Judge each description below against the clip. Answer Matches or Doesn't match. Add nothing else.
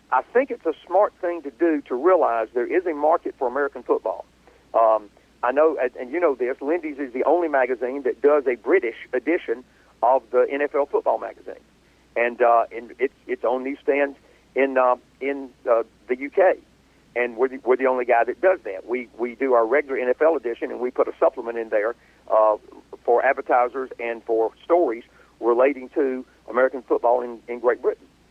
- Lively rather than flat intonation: Matches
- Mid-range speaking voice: Doesn't match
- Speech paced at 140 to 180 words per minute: Doesn't match